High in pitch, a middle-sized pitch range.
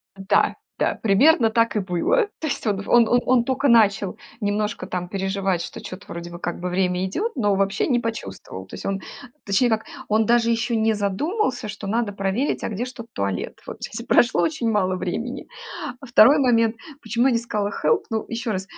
Yes: high, 220 Hz; average, 3.6 semitones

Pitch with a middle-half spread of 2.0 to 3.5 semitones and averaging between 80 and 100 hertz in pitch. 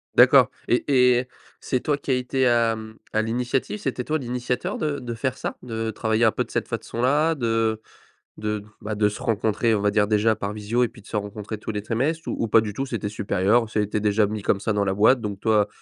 No: average, 2.9 semitones; low, 110 Hz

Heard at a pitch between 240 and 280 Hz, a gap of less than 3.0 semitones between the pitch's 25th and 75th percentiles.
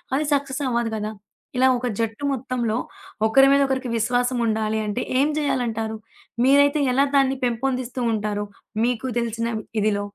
No: high, 245 Hz; average, 3.3 semitones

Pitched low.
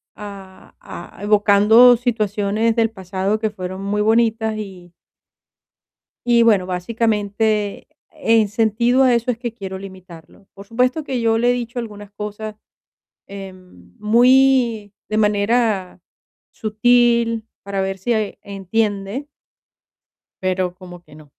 No: high, 210 Hz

